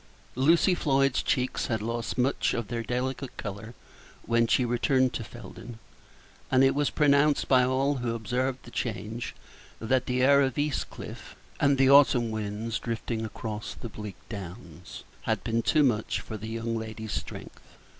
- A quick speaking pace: No, average, 165 wpm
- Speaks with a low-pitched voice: Yes, low, 120 Hz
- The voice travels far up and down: No, average, 3.1 semitones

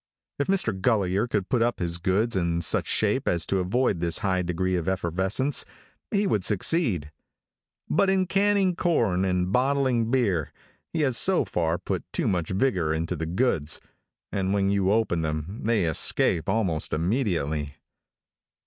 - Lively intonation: Yes, wide, 6.2 semitones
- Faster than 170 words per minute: No, average, 160 wpm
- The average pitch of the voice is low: Yes, very low, 95 Hz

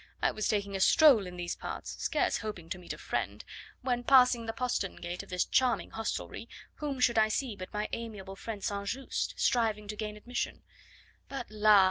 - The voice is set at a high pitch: Yes, high, 215 Hz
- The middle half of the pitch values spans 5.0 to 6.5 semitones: No, average, 3.5 semitones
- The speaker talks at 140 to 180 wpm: No, average, 195 wpm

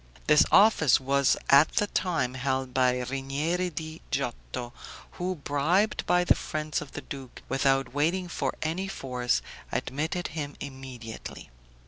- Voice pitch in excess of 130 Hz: Yes, medium, 140 Hz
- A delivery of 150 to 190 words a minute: No, slow, 135 wpm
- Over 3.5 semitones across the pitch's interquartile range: Yes, average, 4.0 semitones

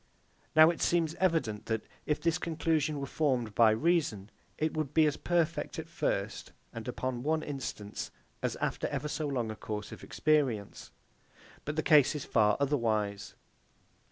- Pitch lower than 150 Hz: Yes, medium, 140 Hz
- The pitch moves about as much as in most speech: No, wide, 5.8 semitones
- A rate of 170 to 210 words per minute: No, average, 160 wpm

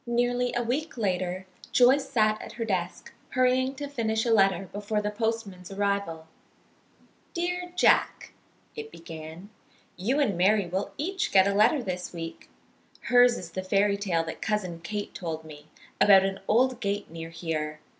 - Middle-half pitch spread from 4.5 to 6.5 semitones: Yes, average, 5.2 semitones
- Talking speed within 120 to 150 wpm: No, average, 160 wpm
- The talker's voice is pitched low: No, high, 205 Hz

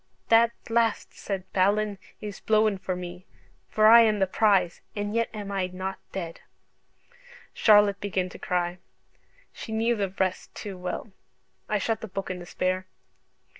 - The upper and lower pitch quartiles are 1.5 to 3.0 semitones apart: Yes, narrow, 2.6 semitones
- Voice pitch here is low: No, high, 200 Hz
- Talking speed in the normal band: Yes, average, 155 wpm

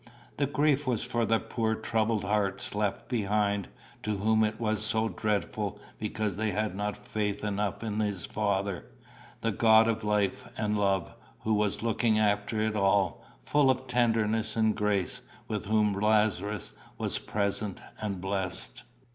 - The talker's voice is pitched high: No, low, 105 Hz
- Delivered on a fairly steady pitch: Yes, narrow, 1.4 semitones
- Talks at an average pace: Yes, average, 155 wpm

